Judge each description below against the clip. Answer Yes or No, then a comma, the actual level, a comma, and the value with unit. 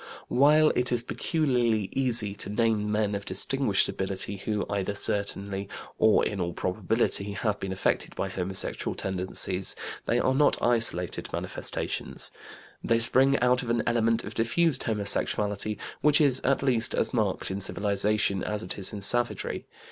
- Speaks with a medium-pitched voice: No, low, 105 Hz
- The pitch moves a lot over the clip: No, average, 3.6 semitones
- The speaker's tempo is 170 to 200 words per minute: No, average, 155 wpm